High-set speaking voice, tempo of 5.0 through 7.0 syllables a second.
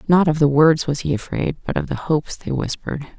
No: medium, 150 Hz; 5.8 syllables/s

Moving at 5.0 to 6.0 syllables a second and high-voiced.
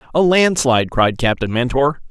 No: 5.2 syllables/s; low, 135 Hz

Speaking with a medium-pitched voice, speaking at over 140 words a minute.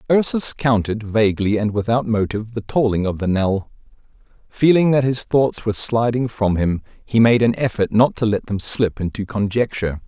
No: low, 110 Hz; average, 180 wpm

